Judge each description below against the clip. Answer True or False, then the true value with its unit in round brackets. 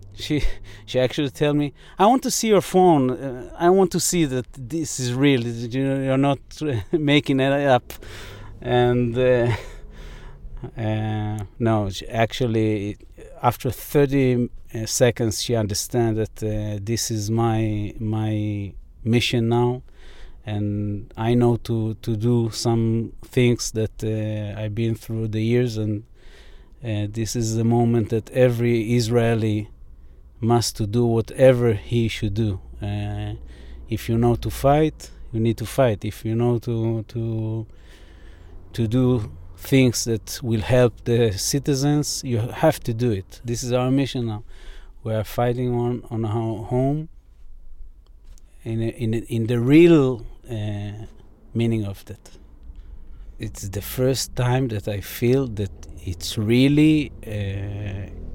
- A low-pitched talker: True (115 Hz)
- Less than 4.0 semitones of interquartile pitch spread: True (3.0 semitones)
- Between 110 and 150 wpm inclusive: True (140 wpm)